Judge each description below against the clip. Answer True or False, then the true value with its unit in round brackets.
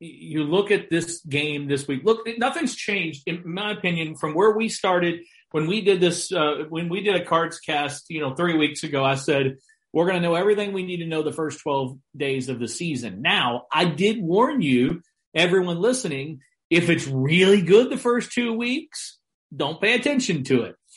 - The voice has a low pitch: False (170 Hz)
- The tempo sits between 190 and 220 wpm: True (205 wpm)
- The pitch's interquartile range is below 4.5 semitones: False (5.1 semitones)